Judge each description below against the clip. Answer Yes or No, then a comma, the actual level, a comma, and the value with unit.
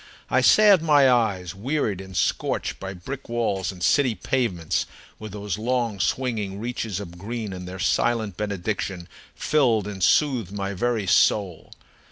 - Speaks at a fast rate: No, average, 150 wpm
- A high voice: No, low, 105 Hz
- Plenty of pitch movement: No, average, 4.2 semitones